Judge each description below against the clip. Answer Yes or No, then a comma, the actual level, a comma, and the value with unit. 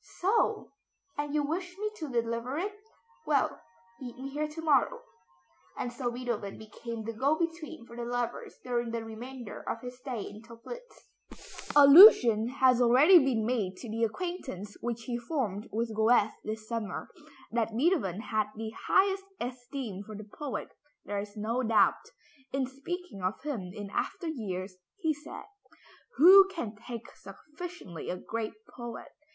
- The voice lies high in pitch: Yes, high, 245 Hz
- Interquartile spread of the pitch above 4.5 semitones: Yes, average, 5.2 semitones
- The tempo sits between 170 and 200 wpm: No, average, 155 wpm